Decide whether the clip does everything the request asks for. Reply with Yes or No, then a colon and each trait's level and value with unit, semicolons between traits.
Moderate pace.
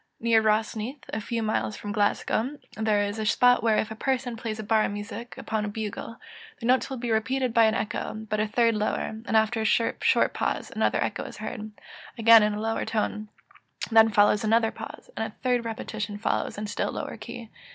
No: fast, 210 wpm